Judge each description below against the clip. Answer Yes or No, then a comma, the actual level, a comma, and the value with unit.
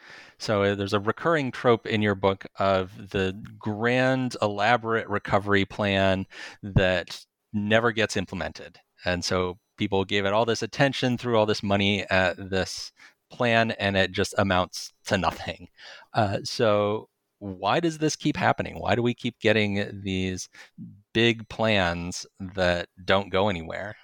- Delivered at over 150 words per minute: No, average, 145 wpm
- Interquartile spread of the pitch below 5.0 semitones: Yes, average, 2.9 semitones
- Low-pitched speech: Yes, low, 105 Hz